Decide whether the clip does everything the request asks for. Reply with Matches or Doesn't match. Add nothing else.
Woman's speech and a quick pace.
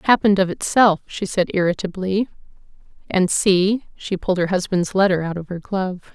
Doesn't match